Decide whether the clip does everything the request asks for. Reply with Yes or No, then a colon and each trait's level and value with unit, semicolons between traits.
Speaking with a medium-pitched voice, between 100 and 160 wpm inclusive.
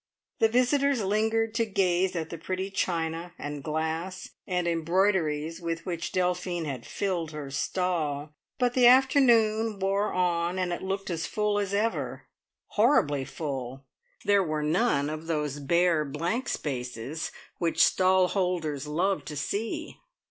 Yes: medium, 180 Hz; average, 140 wpm